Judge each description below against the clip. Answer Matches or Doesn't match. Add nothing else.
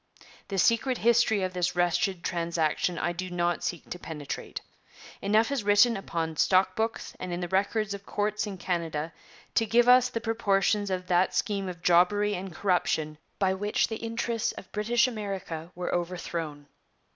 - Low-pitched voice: Doesn't match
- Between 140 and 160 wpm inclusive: Doesn't match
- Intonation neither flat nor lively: Matches